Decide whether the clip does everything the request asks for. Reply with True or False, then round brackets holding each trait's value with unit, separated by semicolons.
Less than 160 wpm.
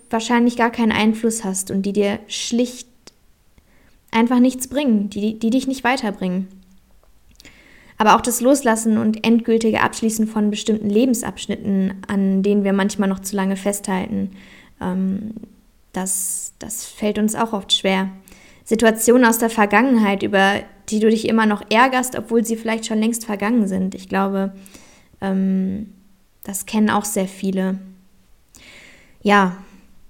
True (140 wpm)